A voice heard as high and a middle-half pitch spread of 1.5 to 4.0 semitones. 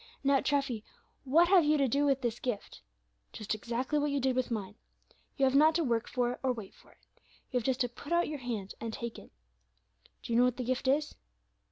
Yes: very high, 255 Hz; average, 3.2 semitones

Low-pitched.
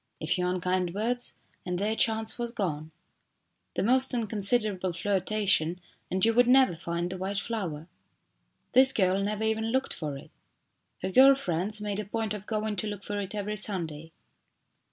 No: high, 205 Hz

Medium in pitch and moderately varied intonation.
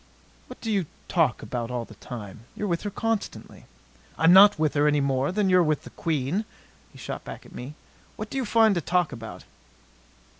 No: medium, 160 Hz; wide, 7.4 semitones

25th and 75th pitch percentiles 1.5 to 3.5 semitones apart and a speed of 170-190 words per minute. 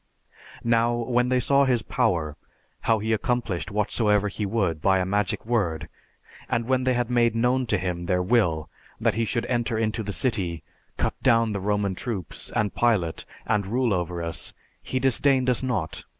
No: average, 4.3 semitones; average, 180 wpm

